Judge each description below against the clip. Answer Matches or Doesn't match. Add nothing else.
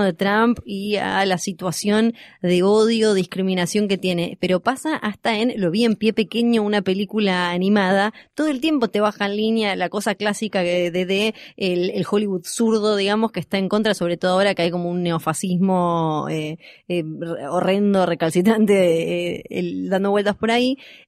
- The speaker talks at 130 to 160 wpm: Doesn't match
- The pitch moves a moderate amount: Matches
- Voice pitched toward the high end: Matches